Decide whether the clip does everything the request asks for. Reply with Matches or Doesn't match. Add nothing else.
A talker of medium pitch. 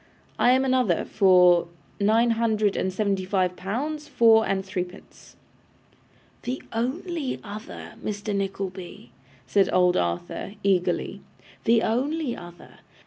Doesn't match